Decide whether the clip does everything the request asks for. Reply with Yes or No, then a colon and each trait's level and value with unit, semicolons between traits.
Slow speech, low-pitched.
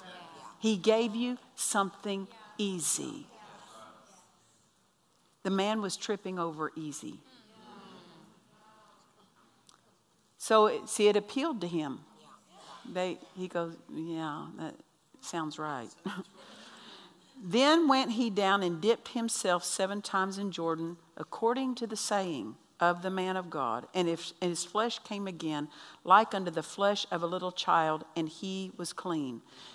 No: slow, 130 wpm; high, 190 Hz